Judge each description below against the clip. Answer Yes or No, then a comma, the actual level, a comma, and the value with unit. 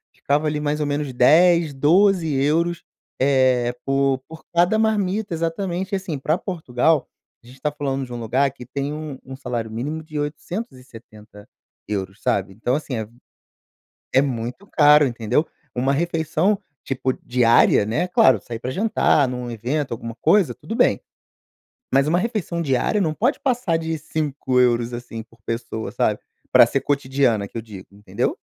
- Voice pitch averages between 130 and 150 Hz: Yes, medium, 140 Hz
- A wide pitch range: No, average, 5.0 semitones